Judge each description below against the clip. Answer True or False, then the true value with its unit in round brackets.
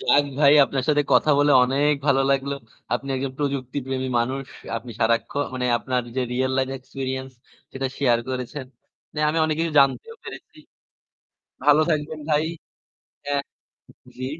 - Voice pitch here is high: False (135 Hz)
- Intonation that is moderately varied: False (2.0 semitones)